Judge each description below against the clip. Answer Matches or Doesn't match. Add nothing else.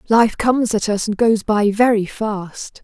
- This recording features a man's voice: Doesn't match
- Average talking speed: Matches